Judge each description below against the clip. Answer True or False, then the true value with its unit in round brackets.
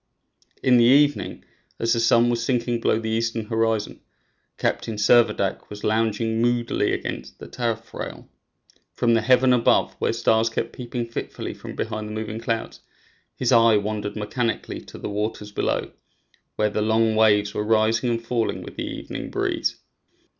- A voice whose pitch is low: True (115 Hz)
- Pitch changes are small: True (1.6 semitones)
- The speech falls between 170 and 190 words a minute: False (160 wpm)